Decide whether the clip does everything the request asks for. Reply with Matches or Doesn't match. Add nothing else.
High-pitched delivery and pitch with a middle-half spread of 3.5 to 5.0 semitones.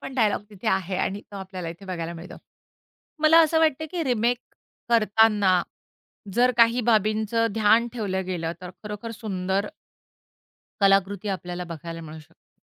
Matches